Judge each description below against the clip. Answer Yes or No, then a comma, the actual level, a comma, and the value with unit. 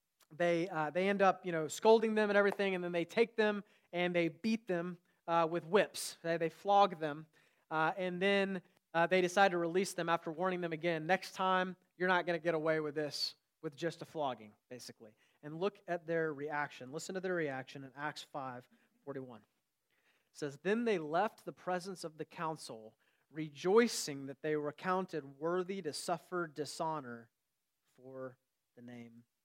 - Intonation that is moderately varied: Yes, average, 3.9 semitones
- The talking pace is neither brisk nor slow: Yes, average, 185 wpm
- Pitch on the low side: No, medium, 165 Hz